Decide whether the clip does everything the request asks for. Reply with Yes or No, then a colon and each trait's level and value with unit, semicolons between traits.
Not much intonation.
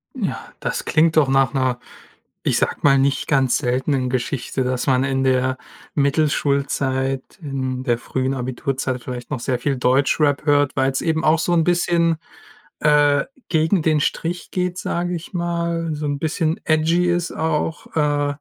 No: average, 3.4 semitones